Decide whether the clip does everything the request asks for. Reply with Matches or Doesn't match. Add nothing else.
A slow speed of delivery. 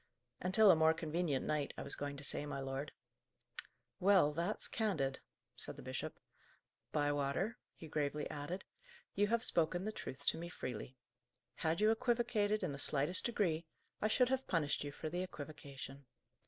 Doesn't match